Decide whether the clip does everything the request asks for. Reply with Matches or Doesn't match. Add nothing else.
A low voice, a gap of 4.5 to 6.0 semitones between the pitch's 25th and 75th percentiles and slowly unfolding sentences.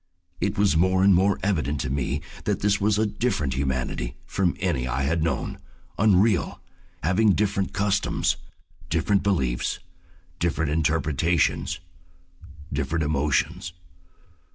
Matches